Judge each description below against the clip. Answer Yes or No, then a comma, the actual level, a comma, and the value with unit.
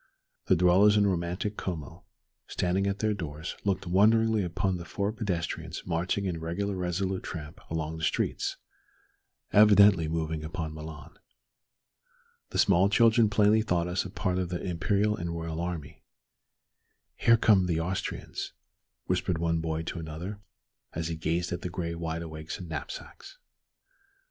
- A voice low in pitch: Yes, very low, 90 Hz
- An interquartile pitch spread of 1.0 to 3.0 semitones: No, average, 3.4 semitones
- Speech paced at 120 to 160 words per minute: Yes, average, 150 wpm